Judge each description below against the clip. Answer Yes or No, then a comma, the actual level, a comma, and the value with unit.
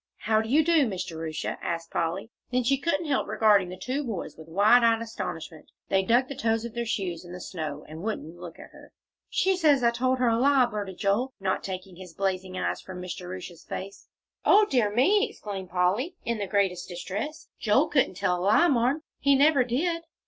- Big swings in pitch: Yes, wide, 5.9 semitones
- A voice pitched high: Yes, high, 215 Hz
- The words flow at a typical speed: No, fast, 210 wpm